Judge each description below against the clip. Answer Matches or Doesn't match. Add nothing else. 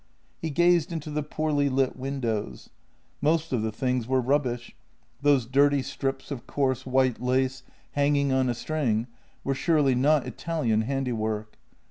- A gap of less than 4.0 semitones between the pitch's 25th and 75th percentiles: Matches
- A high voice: Doesn't match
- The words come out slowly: Doesn't match